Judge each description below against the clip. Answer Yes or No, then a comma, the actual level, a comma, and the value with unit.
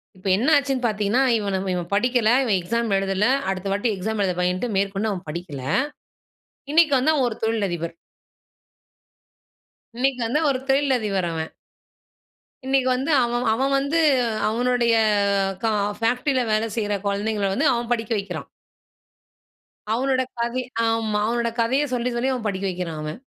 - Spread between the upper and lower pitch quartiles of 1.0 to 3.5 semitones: No, average, 4.2 semitones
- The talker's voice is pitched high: Yes, high, 225 Hz